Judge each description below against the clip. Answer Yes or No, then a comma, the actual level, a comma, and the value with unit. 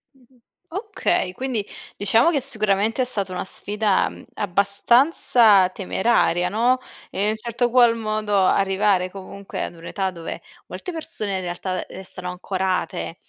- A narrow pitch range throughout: No, average, 4.0 semitones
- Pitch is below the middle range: No, high, 205 Hz